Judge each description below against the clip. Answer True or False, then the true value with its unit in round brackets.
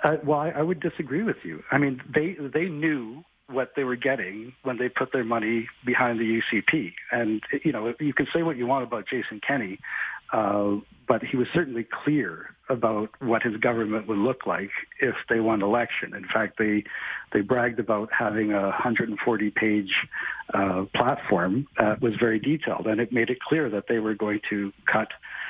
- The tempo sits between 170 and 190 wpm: True (185 wpm)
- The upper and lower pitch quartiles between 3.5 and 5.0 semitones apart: True (4.1 semitones)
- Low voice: True (120 Hz)